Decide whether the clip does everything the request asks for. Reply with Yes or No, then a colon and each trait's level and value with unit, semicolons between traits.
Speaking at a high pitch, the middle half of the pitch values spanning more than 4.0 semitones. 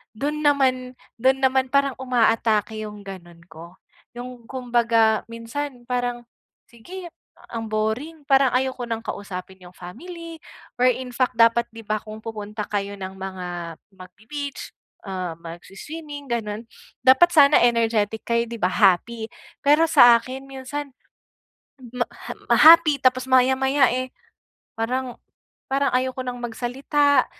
No: high, 245 Hz; average, 3.7 semitones